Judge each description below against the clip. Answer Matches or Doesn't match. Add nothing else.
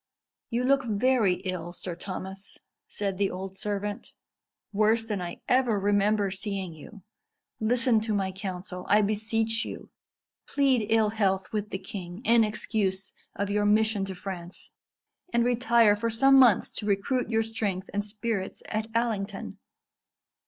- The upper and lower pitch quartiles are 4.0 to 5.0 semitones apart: Doesn't match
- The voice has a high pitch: Matches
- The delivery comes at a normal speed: Matches